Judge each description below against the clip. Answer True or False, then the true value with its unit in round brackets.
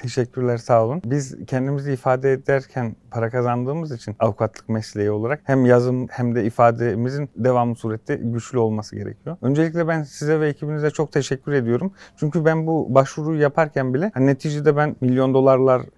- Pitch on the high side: False (130 Hz)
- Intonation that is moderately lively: True (3.9 semitones)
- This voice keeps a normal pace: False (160 wpm)